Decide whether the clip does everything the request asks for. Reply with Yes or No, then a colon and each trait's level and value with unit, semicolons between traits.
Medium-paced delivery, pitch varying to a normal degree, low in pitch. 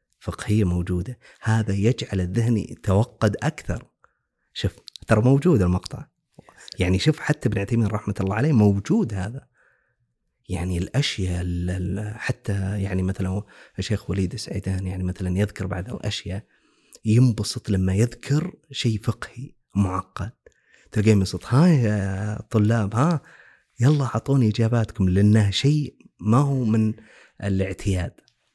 Yes: average, 115 wpm; average, 4.3 semitones; low, 105 Hz